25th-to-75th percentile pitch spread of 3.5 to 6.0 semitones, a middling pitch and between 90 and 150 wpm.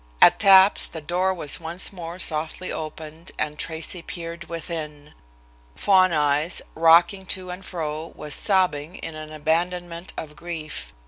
No: average, 2.7 semitones; medium, 165 Hz; average, 140 wpm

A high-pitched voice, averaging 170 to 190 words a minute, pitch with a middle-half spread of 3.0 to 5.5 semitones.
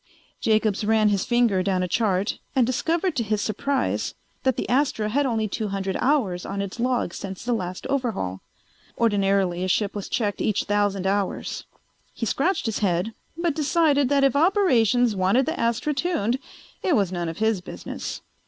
Yes: high, 220 Hz; average, 175 wpm; average, 5.0 semitones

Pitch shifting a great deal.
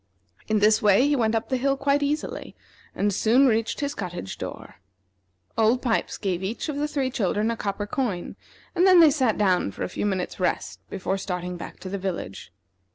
Yes: wide, 6.0 semitones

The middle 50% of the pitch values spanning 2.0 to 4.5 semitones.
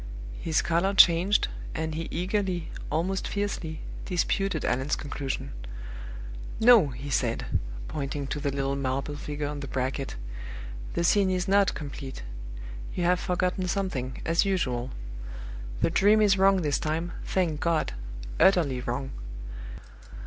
No: average, 5.1 semitones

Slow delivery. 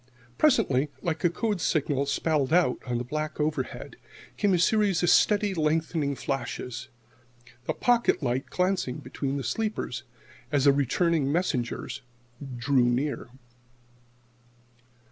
Yes: slow, 125 wpm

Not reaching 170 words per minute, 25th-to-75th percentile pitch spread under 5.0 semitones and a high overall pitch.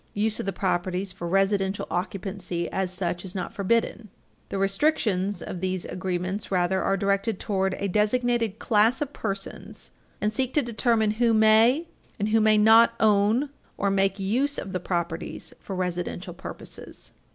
Yes: average, 160 wpm; average, 2.9 semitones; high, 200 Hz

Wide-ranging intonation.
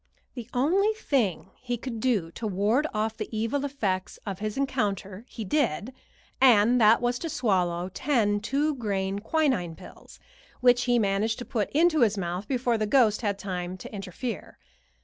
No: average, 4.4 semitones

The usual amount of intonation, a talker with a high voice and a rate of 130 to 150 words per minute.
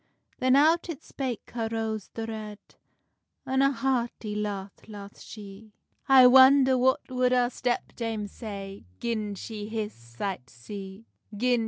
Yes: average, 3.7 semitones; high, 225 Hz; average, 145 wpm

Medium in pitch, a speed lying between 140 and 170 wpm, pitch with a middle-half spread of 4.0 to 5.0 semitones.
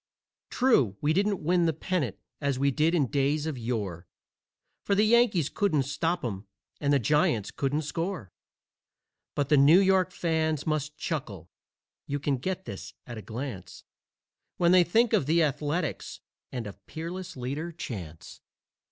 No: medium, 150 Hz; average, 155 wpm; wide, 5.5 semitones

